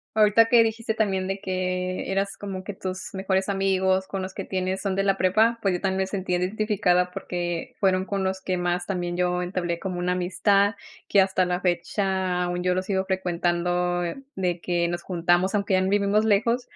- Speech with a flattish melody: Yes, narrow, 1.7 semitones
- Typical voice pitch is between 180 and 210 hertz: Yes, high, 190 Hz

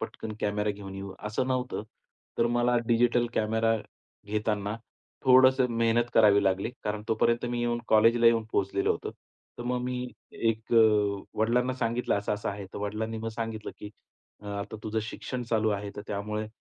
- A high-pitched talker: No, low, 110 Hz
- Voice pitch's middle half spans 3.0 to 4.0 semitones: No, narrow, 2.4 semitones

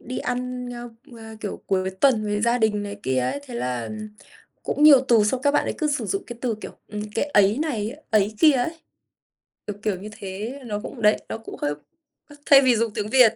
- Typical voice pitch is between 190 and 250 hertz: Yes, high, 225 Hz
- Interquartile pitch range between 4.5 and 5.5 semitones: No, average, 3.8 semitones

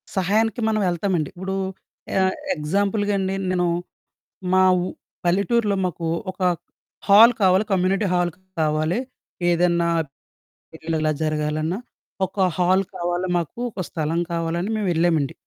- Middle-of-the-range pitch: Yes, medium, 180 Hz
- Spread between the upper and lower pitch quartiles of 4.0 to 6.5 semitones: No, average, 2.9 semitones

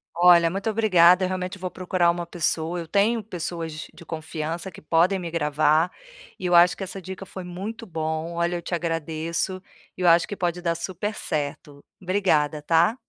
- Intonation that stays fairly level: Yes, narrow, 2.3 semitones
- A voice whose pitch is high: No, medium, 175 Hz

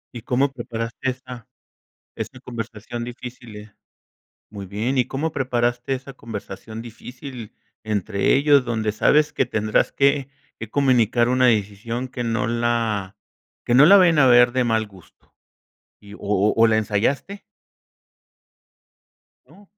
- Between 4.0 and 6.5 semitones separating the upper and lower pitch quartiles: No, average, 3.0 semitones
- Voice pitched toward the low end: Yes, low, 120 Hz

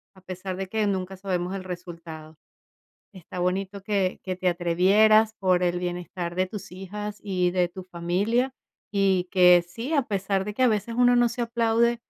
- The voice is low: No, high, 190 Hz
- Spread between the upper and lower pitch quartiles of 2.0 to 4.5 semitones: Yes, average, 2.9 semitones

